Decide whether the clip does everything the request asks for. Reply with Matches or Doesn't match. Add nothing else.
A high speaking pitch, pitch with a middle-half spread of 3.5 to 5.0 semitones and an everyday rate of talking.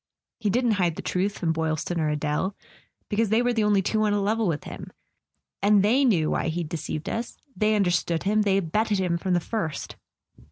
Doesn't match